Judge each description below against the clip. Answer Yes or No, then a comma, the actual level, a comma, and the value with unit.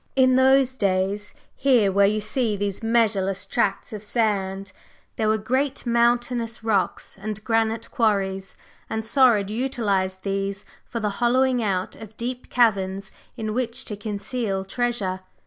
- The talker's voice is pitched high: Yes, high, 215 Hz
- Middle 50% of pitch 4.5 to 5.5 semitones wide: No, average, 3.4 semitones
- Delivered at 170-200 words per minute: No, average, 140 wpm